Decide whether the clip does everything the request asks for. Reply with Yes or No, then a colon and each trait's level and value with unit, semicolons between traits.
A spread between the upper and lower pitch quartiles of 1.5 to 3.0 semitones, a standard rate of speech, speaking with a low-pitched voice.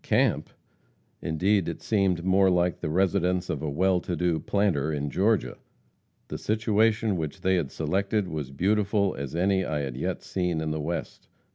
No: average, 3.9 semitones; average, 170 wpm; very low, 90 Hz